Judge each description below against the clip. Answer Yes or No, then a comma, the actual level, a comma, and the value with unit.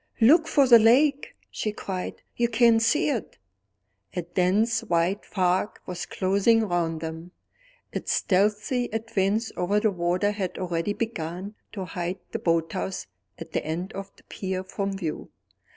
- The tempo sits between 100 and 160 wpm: Yes, average, 150 wpm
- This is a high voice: Yes, high, 195 Hz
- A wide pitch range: No, average, 4.0 semitones